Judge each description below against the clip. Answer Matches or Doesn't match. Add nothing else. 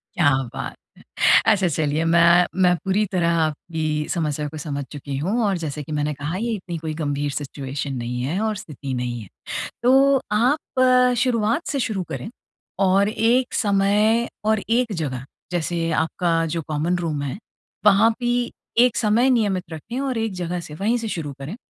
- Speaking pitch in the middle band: Matches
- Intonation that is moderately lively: Doesn't match